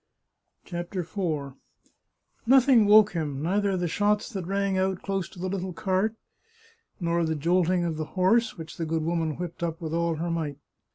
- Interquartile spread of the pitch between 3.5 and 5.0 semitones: No, average, 3.1 semitones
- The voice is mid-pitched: Yes, medium, 175 Hz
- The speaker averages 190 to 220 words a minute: No, average, 175 wpm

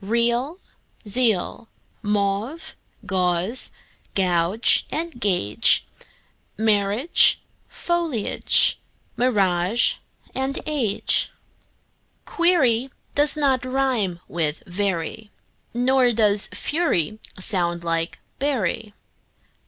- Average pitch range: No, wide, 6.0 semitones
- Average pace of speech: No, slow, 65 wpm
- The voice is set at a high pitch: Yes, high, 220 Hz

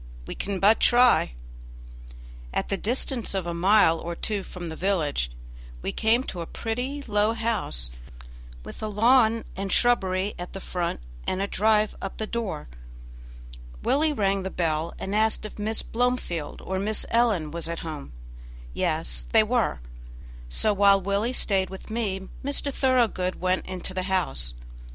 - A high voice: Yes, high, 195 Hz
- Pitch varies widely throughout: No, average, 4.0 semitones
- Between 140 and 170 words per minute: Yes, average, 160 wpm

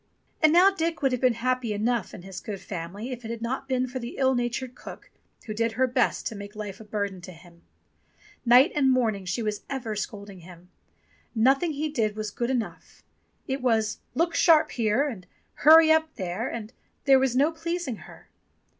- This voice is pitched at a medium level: No, high, 240 Hz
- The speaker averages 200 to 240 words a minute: Yes, fast, 205 wpm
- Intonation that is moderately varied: Yes, average, 4.3 semitones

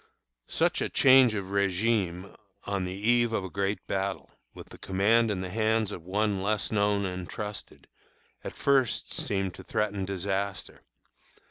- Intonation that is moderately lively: No, narrow, 2.2 semitones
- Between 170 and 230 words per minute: No, average, 155 wpm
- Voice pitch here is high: No, low, 100 Hz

